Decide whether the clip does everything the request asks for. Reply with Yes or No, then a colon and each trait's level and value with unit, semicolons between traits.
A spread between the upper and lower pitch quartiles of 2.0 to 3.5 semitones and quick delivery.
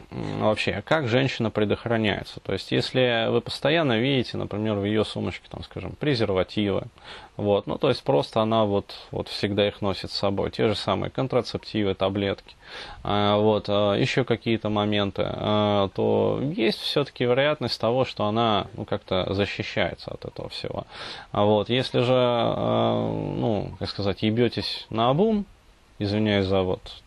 No: average, 2.8 semitones; average, 140 wpm